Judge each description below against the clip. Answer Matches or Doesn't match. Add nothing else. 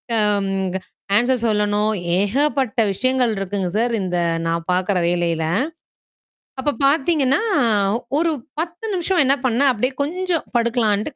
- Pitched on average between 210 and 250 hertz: Matches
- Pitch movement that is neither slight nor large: Doesn't match